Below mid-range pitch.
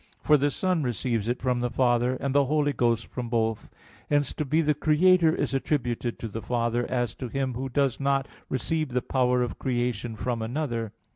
Yes: low, 125 Hz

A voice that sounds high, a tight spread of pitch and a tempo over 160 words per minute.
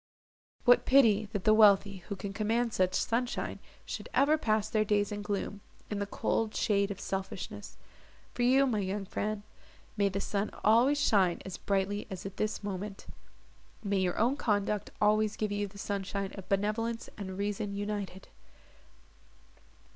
No: high, 205 Hz; narrow, 1.6 semitones; average, 155 wpm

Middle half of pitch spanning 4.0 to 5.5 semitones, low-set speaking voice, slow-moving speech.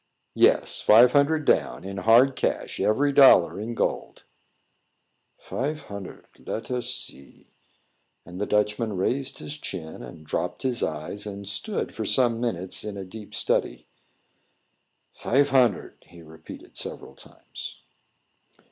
Yes: average, 5.1 semitones; low, 110 Hz; slow, 130 wpm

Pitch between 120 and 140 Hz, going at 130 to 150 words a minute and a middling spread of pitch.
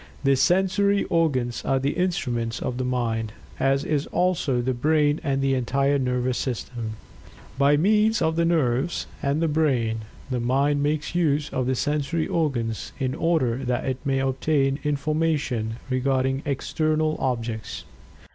Yes: low, 135 Hz; average, 145 wpm; average, 3.7 semitones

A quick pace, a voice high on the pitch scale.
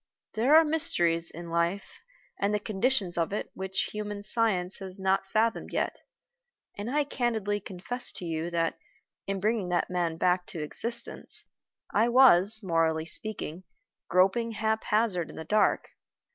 No: average, 145 wpm; high, 195 Hz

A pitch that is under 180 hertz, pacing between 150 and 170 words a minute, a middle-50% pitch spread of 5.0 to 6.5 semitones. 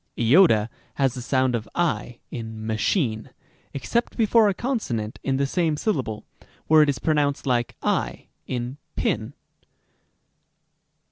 No: low, 135 Hz; slow, 135 wpm; wide, 5.4 semitones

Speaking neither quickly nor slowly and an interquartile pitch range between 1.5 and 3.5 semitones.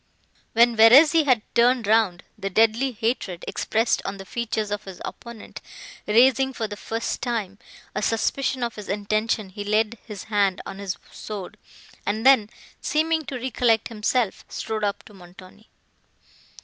Yes: average, 150 wpm; average, 2.7 semitones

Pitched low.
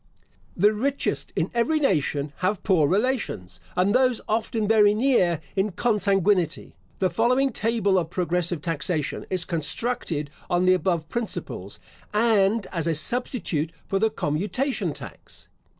No: high, 195 Hz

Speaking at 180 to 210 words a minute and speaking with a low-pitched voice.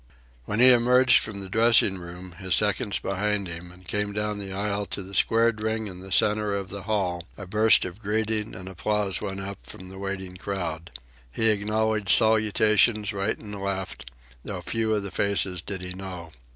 Yes: average, 190 wpm; low, 100 Hz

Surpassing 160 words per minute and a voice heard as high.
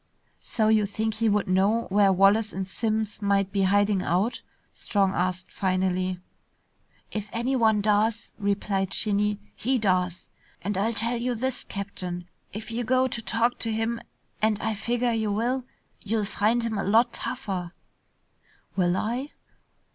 No: average, 150 wpm; high, 210 Hz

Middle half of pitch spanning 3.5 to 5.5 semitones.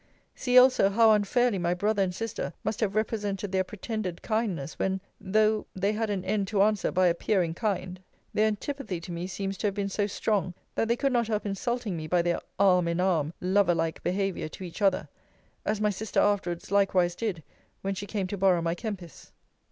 No: average, 3.1 semitones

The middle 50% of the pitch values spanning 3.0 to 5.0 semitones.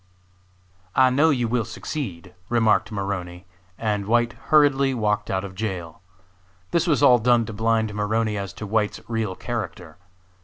Yes: average, 3.3 semitones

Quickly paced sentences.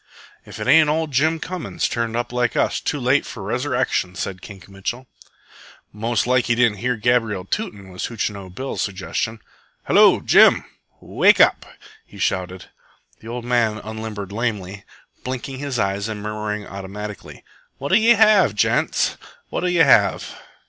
No: average, 150 wpm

